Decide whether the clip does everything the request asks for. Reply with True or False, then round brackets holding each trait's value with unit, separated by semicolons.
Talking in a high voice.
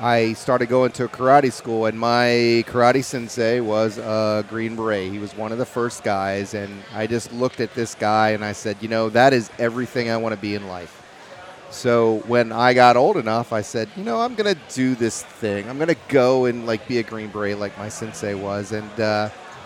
False (115 Hz)